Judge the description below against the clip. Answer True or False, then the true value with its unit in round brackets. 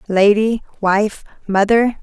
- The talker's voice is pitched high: True (210 Hz)